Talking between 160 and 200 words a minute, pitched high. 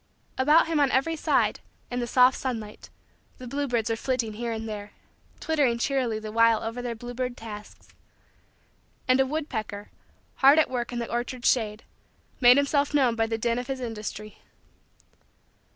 Yes: average, 165 wpm; high, 245 Hz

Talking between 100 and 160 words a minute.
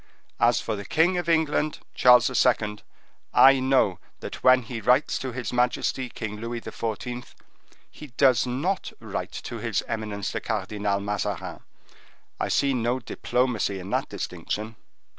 Yes: average, 145 wpm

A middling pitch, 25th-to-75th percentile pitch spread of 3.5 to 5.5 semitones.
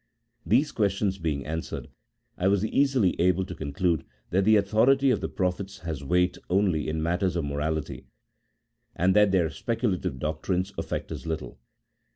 No: very low, 90 Hz; average, 4.1 semitones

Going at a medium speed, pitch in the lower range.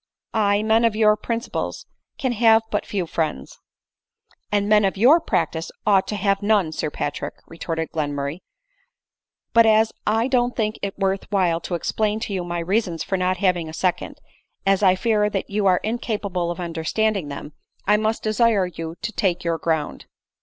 No: average, 185 wpm; high, 200 Hz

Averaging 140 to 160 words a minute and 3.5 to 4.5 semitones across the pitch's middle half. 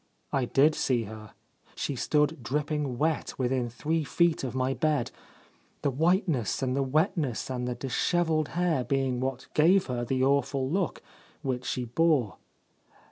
Yes: average, 150 wpm; average, 3.8 semitones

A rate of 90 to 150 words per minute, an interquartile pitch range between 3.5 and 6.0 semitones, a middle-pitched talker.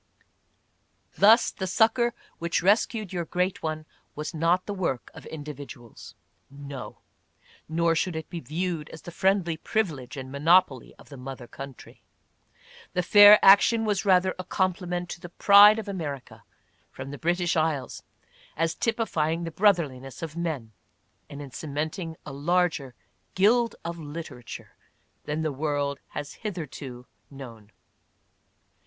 Yes: average, 140 wpm; average, 4.6 semitones; medium, 165 Hz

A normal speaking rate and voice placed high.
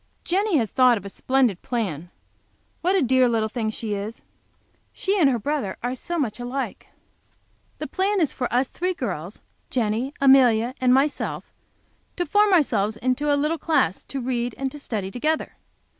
Yes: average, 175 wpm; very high, 255 Hz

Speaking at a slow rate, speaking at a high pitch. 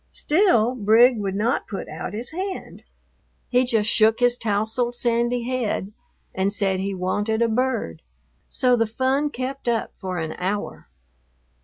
No: average, 150 wpm; high, 230 Hz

